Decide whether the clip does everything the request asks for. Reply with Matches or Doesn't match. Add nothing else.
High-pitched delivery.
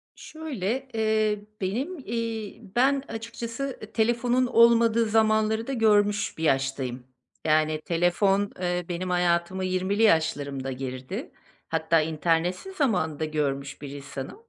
Matches